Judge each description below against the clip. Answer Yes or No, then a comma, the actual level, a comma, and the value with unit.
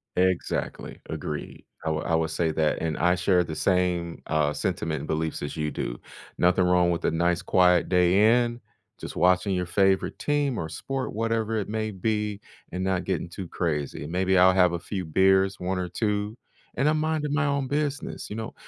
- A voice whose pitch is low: Yes, very low, 90 Hz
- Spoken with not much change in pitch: No, average, 4.0 semitones